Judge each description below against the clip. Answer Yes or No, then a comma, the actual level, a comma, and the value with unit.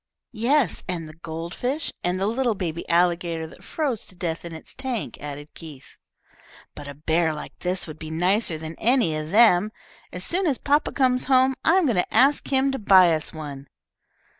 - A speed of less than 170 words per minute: No, average, 195 wpm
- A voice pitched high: No, medium, 180 Hz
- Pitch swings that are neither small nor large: No, wide, 7.9 semitones